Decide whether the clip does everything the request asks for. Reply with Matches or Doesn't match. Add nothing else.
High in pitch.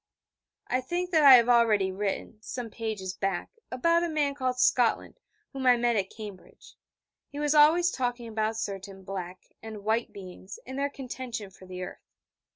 Matches